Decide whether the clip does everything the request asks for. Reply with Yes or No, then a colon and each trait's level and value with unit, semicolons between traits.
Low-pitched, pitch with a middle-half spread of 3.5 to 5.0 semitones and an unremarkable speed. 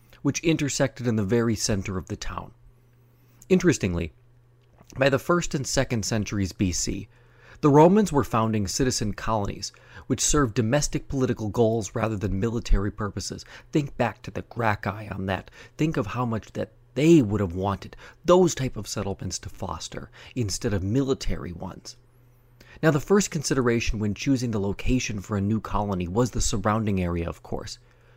Yes: low, 115 Hz; average, 4.0 semitones; average, 160 wpm